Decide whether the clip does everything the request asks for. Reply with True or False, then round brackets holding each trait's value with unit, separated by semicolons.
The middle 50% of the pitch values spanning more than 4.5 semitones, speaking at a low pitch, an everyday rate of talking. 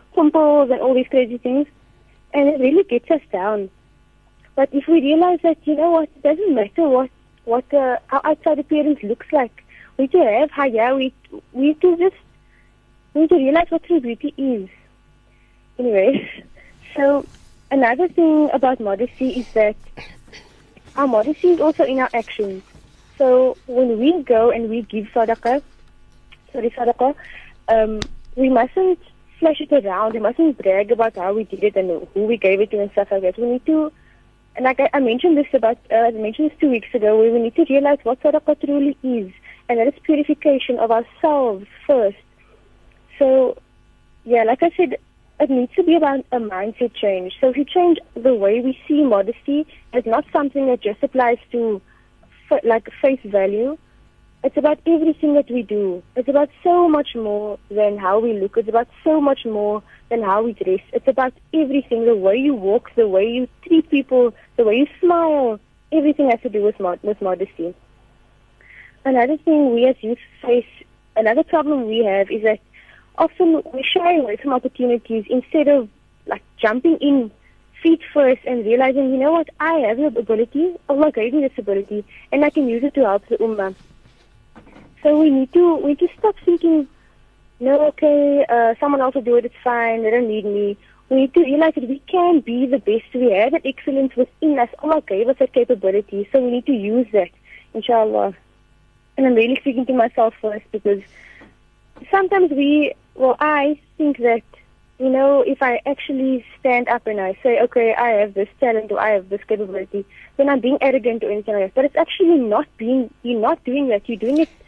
False (4.9 semitones; 255 Hz; 190 wpm)